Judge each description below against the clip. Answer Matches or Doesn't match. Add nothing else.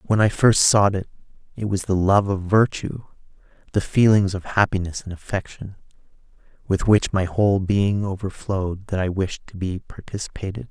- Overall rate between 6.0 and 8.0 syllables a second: Doesn't match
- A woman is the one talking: Doesn't match